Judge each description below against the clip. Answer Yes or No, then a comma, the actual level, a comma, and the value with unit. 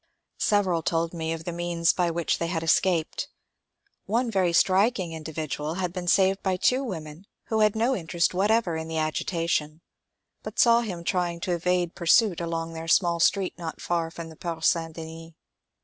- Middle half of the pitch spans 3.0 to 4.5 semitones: No, narrow, 2.5 semitones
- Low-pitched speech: No, medium, 170 Hz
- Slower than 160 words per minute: No, average, 180 wpm